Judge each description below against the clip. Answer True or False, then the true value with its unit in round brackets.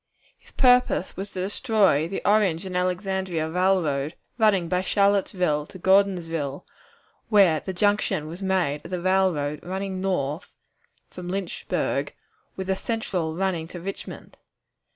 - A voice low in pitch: False (185 Hz)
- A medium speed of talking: False (130 wpm)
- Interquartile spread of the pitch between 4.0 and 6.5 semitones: False (2.9 semitones)